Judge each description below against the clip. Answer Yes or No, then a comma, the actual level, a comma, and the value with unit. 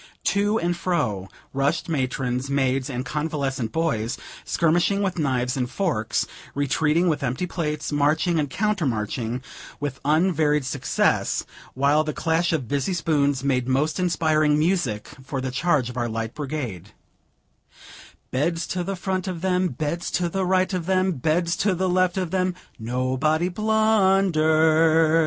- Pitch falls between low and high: Yes, medium, 155 Hz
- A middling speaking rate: Yes, average, 145 wpm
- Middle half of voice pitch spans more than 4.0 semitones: Yes, average, 5.1 semitones